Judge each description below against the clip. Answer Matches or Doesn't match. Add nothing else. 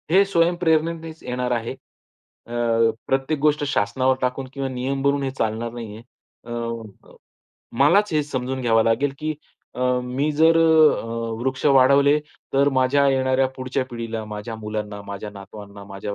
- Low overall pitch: Matches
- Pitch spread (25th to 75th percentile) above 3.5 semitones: Matches